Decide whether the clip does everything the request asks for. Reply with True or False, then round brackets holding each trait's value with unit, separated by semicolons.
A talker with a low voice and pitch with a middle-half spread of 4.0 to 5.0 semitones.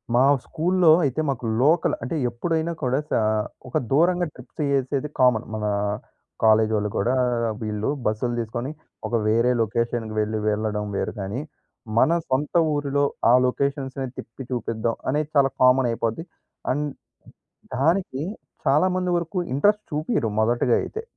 True (130 Hz; 4.7 semitones)